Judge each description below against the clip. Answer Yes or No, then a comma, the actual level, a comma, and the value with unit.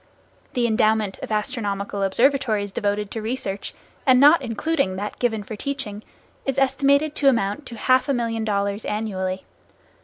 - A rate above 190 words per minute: No, average, 150 wpm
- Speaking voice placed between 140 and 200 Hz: No, high, 220 Hz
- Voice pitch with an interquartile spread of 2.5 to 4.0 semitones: No, average, 4.4 semitones